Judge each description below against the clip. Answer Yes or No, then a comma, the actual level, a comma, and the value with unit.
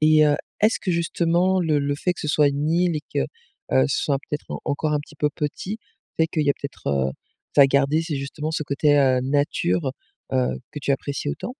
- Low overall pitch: No, medium, 150 Hz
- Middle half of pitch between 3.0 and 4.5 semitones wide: No, narrow, 2.6 semitones